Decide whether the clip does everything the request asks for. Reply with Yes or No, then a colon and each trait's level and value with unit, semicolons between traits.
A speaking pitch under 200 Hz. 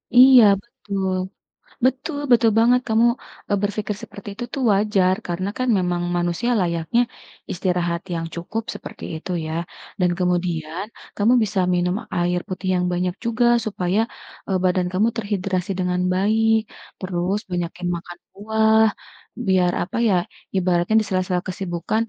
Yes: medium, 185 Hz